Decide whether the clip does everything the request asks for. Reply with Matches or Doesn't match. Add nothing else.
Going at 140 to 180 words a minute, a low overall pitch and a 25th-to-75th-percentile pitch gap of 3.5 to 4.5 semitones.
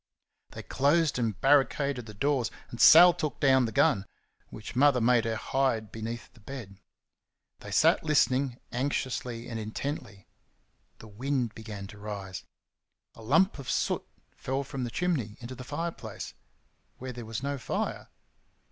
Matches